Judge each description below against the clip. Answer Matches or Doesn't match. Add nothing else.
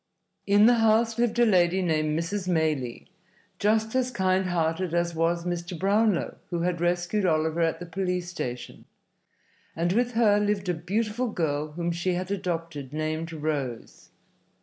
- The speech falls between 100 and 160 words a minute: Matches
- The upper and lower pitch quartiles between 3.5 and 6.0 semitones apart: Matches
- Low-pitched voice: Doesn't match